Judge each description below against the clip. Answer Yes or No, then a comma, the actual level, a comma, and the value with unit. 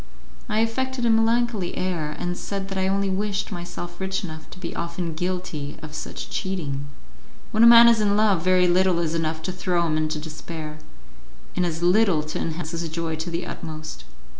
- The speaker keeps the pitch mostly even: No, average, 3.6 semitones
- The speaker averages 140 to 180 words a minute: No, average, 190 wpm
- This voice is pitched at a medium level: Yes, medium, 175 Hz